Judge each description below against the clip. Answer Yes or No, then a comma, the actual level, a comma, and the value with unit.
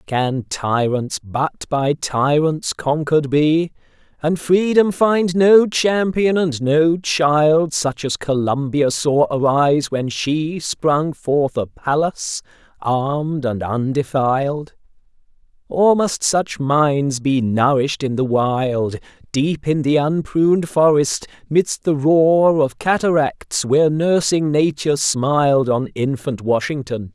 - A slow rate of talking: Yes, slow, 120 wpm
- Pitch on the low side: No, medium, 145 Hz